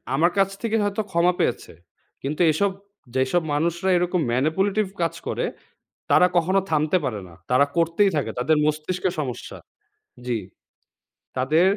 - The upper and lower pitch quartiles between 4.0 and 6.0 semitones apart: Yes, average, 4.5 semitones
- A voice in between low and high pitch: Yes, medium, 165 Hz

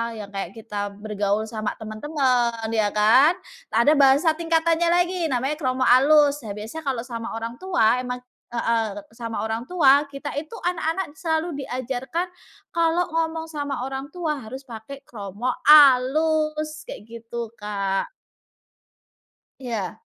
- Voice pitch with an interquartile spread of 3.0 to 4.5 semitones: No, wide, 5.5 semitones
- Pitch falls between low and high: No, very high, 260 Hz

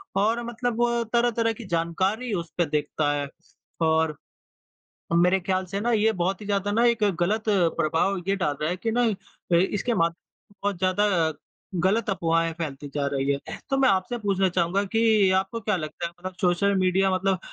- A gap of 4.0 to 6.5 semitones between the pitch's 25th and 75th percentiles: Yes, average, 4.3 semitones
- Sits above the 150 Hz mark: Yes, high, 190 Hz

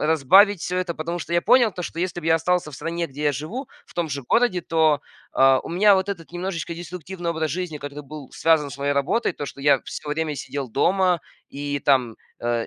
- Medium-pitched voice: Yes, medium, 160 Hz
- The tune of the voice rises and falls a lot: No, average, 3.9 semitones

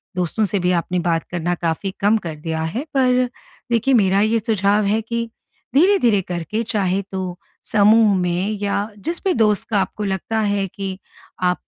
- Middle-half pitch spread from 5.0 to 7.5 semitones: No, average, 3.7 semitones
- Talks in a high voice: Yes, high, 200 Hz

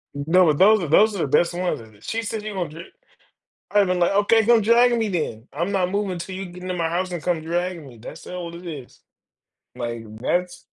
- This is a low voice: No, medium, 180 Hz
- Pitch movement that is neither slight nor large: Yes, average, 3.6 semitones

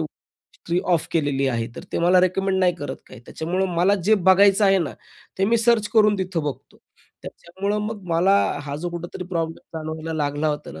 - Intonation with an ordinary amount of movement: Yes, average, 3.6 semitones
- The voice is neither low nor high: Yes, medium, 175 Hz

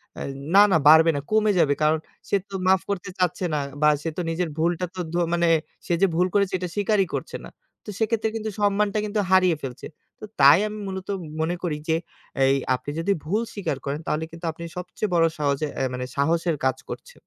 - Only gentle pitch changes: No, average, 4.1 semitones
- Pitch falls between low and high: Yes, medium, 175 Hz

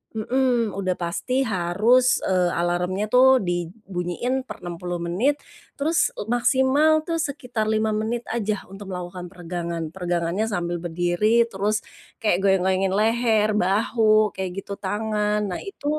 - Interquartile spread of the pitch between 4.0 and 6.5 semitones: Yes, average, 4.5 semitones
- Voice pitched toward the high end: Yes, high, 205 Hz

